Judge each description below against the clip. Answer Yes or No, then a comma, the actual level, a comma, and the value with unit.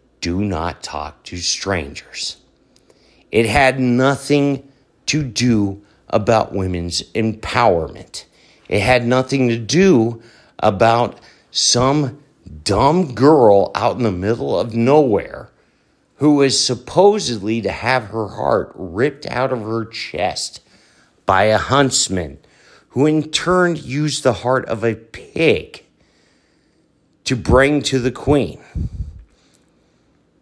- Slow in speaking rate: Yes, slow, 110 wpm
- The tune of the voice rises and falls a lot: No, average, 5.0 semitones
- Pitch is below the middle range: Yes, low, 120 Hz